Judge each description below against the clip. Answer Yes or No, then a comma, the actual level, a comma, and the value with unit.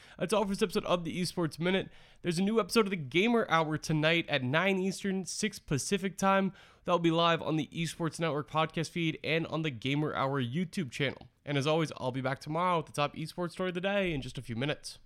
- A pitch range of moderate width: Yes, average, 4.0 semitones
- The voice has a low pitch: No, medium, 165 Hz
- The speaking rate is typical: No, fast, 245 wpm